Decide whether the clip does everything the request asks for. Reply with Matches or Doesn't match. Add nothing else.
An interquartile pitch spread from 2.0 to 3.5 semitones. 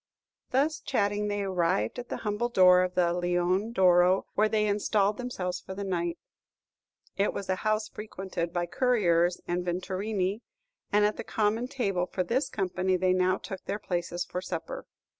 Matches